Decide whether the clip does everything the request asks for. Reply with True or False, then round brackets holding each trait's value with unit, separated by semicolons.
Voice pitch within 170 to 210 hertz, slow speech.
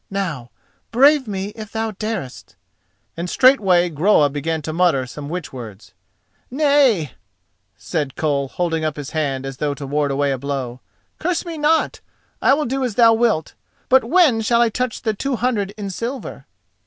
False (190 Hz; 170 wpm)